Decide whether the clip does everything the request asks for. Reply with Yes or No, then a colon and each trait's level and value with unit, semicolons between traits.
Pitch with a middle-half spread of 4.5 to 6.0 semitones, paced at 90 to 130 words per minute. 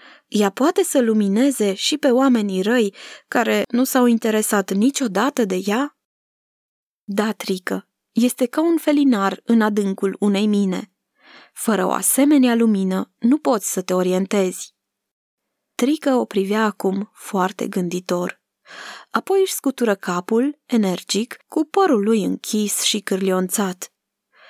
Yes: average, 4.9 semitones; average, 125 wpm